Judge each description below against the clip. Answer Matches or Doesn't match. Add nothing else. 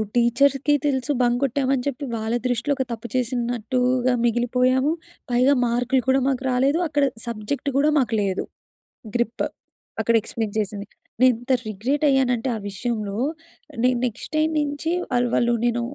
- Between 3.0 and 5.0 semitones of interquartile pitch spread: Doesn't match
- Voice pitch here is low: Doesn't match